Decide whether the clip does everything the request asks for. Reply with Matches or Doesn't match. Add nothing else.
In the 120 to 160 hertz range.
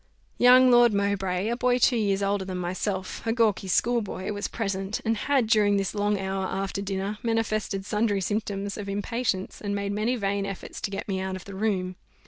Doesn't match